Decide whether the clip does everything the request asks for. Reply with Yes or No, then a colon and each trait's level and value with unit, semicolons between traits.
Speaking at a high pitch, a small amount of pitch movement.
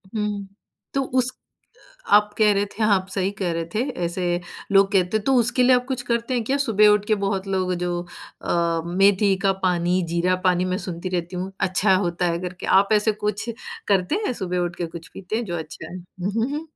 No: high, 195 Hz; average, 3.2 semitones